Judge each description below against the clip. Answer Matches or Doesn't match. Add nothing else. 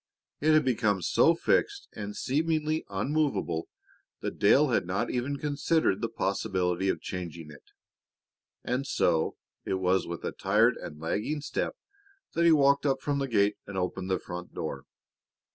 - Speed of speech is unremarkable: Matches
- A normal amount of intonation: Doesn't match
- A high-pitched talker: Doesn't match